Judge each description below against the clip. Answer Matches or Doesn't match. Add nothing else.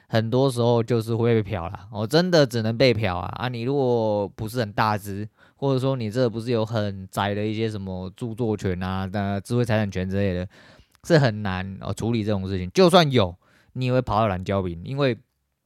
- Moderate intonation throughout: Matches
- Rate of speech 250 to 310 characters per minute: Matches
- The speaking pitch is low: Matches